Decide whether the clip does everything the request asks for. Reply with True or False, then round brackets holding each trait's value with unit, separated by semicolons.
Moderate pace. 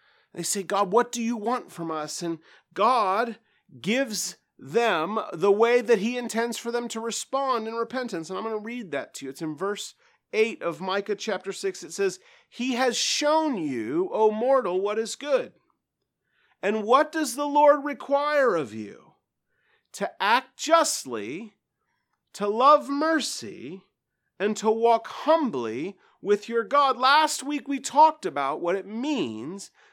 True (160 wpm)